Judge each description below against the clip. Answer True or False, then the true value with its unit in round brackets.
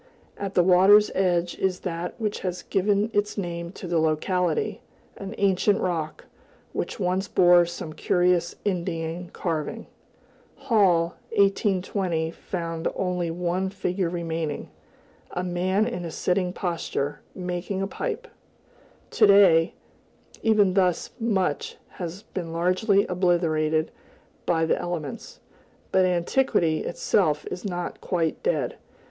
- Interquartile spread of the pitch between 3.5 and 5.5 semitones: False (2.4 semitones)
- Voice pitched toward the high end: False (180 Hz)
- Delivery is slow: True (120 wpm)